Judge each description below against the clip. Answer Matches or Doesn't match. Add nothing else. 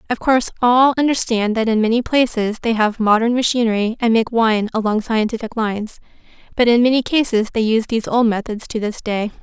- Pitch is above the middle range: Matches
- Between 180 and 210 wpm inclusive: Matches